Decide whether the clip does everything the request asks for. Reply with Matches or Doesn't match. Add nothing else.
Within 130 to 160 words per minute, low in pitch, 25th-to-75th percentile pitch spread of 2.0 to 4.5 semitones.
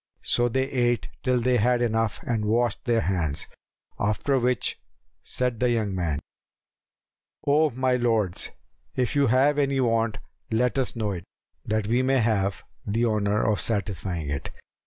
Matches